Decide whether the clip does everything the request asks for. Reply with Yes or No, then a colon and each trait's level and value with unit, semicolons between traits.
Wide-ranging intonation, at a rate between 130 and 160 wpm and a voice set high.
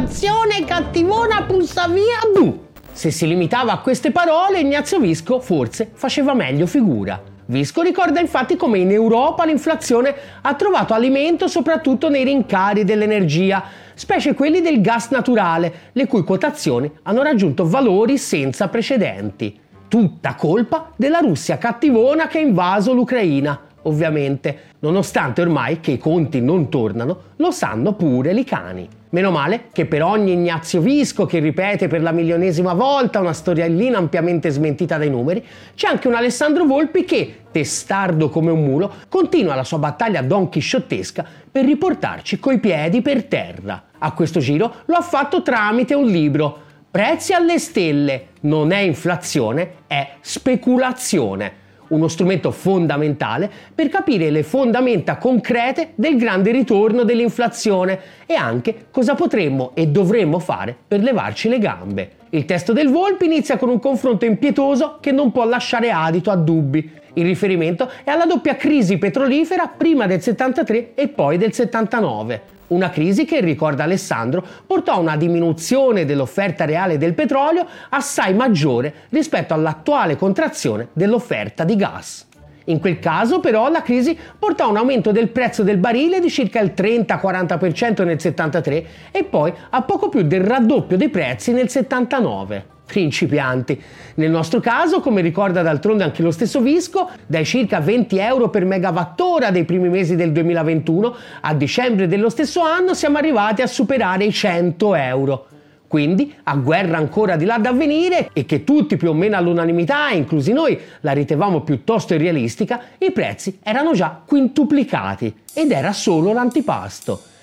Yes: wide, 8.6 semitones; average, 150 wpm; high, 205 Hz